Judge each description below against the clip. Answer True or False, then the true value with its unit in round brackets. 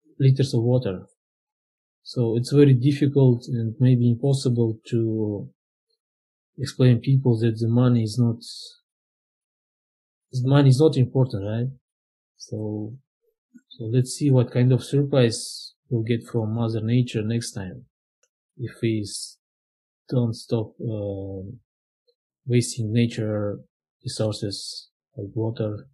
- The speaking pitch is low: True (120 Hz)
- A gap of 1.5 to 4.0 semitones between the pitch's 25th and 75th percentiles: True (3.3 semitones)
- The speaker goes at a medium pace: False (115 wpm)